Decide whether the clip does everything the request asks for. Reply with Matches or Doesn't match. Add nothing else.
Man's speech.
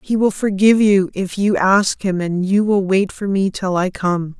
Doesn't match